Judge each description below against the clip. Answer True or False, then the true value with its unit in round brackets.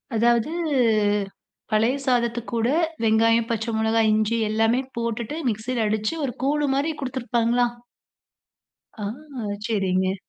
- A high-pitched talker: True (230 Hz)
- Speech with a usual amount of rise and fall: False (1.9 semitones)